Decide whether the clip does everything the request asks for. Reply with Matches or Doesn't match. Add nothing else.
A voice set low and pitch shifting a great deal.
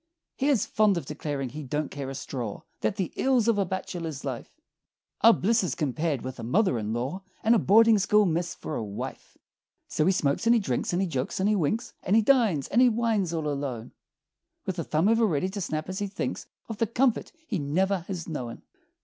Doesn't match